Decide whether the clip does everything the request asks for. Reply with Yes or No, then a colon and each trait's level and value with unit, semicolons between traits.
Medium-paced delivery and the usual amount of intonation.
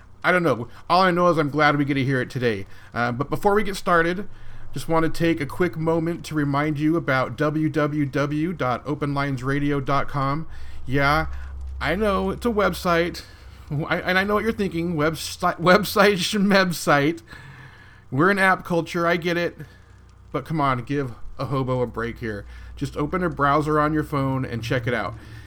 Yes: average, 180 wpm; average, 4.9 semitones